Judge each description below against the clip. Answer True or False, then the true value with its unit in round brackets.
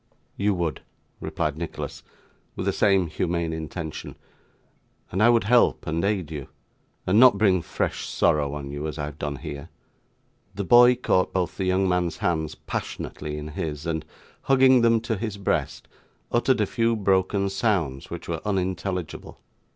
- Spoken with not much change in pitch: False (4.7 semitones)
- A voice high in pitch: False (90 Hz)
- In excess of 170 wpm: False (160 wpm)